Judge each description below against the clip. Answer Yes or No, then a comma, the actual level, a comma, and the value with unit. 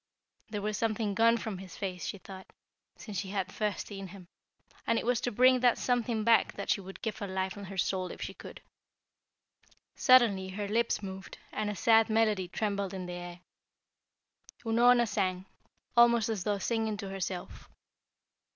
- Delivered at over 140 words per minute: Yes, average, 180 wpm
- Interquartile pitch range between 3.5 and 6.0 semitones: No, average, 3.1 semitones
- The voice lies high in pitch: Yes, high, 205 Hz